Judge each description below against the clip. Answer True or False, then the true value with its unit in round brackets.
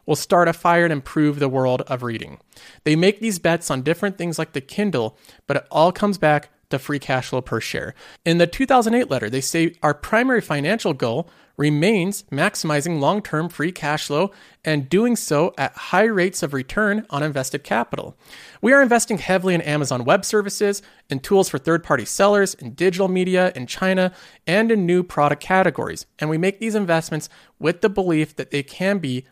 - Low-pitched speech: False (170 Hz)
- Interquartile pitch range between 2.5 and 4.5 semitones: False (5.2 semitones)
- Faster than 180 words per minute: True (190 wpm)